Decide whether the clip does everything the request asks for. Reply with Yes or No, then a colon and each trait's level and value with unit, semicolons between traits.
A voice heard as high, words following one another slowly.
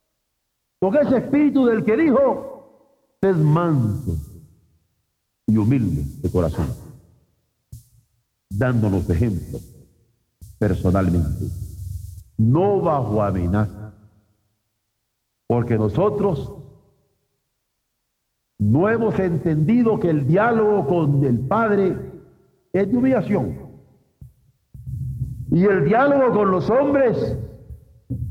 No: low, 125 Hz; slow, 80 wpm